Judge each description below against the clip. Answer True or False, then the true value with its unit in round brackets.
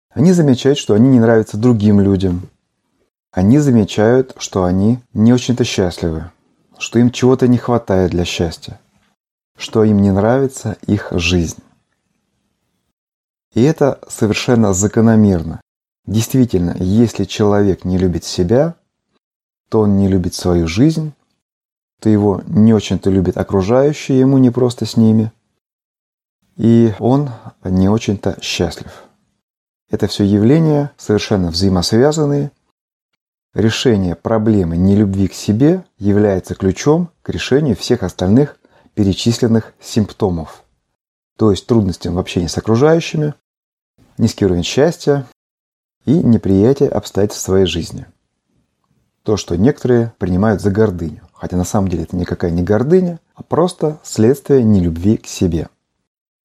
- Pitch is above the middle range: False (110 Hz)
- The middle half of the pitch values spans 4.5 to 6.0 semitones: True (4.8 semitones)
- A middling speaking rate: True (120 wpm)